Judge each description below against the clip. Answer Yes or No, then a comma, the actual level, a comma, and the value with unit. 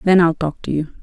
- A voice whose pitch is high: No, medium, 165 Hz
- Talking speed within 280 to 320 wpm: Yes, fast, 290 wpm